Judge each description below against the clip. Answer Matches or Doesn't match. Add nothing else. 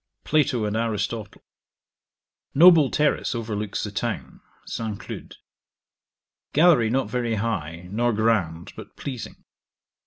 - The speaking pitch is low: Matches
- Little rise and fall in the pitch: Doesn't match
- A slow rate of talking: Matches